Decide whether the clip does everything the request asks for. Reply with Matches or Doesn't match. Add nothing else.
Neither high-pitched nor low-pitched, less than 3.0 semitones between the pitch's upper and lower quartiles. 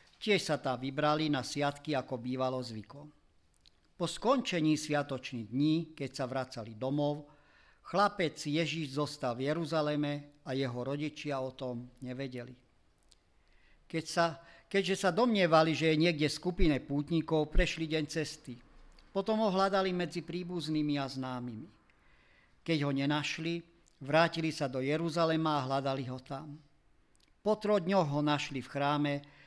Doesn't match